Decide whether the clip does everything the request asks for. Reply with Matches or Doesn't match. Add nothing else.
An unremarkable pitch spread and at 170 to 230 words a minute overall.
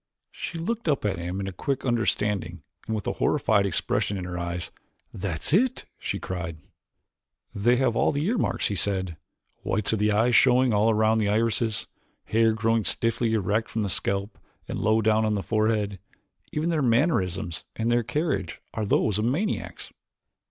Matches